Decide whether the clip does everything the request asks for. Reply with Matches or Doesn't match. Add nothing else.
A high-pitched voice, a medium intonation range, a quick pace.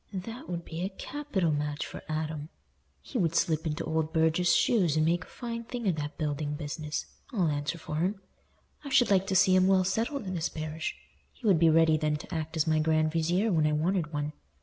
Doesn't match